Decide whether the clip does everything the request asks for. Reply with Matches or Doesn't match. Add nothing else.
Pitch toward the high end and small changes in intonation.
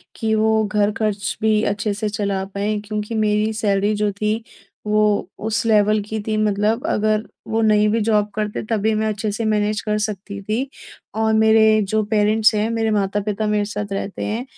Matches